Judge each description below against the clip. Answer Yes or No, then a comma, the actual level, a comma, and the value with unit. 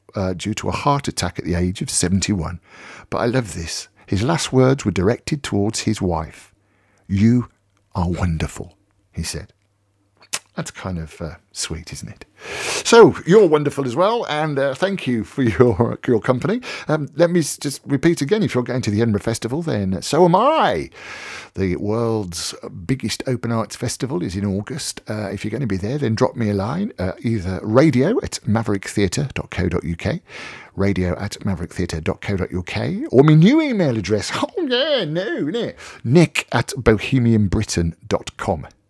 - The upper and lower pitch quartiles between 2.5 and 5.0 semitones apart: No, wide, 5.6 semitones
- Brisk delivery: No, average, 165 wpm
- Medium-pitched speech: No, low, 110 Hz